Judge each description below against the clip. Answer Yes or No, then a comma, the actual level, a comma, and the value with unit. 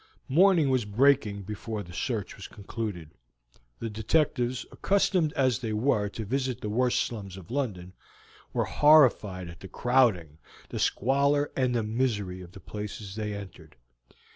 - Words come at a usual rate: Yes, average, 150 wpm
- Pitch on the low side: Yes, low, 110 Hz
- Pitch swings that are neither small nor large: Yes, average, 4.8 semitones